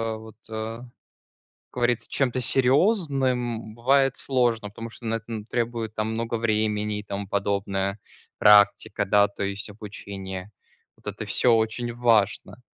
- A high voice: No, low, 110 Hz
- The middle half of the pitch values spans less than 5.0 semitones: Yes, average, 2.7 semitones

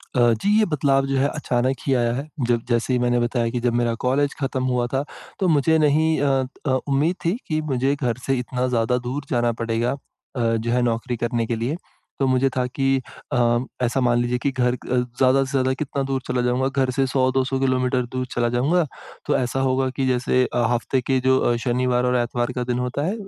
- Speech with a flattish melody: Yes, narrow, 1.9 semitones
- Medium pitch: No, low, 130 Hz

